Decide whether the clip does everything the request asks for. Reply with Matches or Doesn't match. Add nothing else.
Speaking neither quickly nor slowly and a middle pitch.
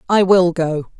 Matches